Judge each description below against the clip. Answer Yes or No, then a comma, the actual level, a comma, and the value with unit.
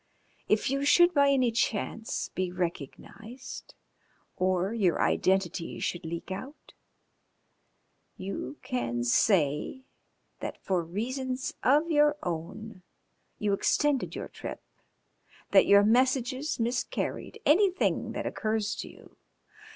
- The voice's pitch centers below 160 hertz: No, high, 220 Hz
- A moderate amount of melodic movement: No, wide, 6.4 semitones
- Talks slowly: Yes, slow, 110 wpm